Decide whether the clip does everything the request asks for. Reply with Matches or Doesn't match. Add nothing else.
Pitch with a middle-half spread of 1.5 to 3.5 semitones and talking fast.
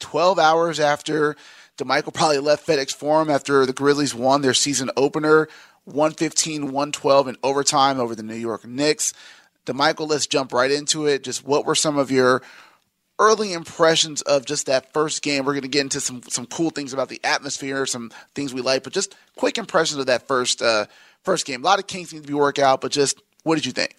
Matches